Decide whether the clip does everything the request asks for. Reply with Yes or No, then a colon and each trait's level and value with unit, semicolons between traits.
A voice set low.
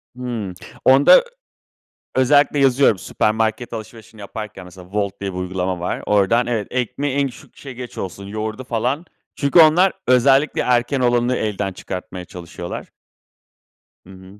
Yes: low, 115 Hz